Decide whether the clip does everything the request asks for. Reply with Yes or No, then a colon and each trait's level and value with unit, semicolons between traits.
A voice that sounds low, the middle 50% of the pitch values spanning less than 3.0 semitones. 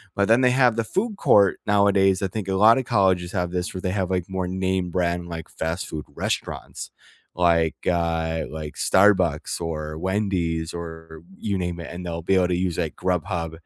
Yes: very low, 90 Hz; narrow, 2.6 semitones